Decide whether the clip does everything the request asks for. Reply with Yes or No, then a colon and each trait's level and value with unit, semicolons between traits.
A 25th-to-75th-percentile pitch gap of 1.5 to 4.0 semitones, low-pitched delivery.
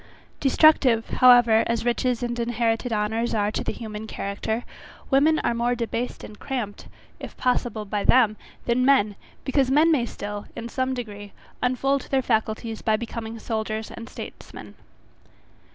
No: narrow, 2.6 semitones; high, 235 Hz